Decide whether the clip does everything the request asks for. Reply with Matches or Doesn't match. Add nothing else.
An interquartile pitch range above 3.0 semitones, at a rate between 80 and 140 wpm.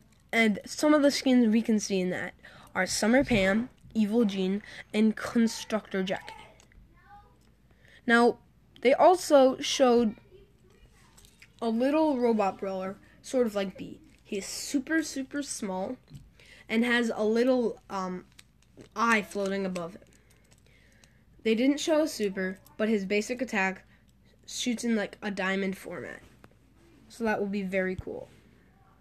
Matches